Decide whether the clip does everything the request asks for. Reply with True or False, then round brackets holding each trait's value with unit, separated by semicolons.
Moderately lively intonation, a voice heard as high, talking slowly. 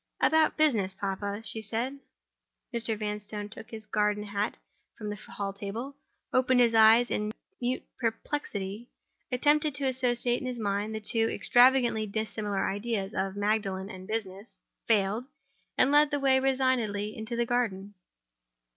True (3.4 semitones; 220 Hz; 130 wpm)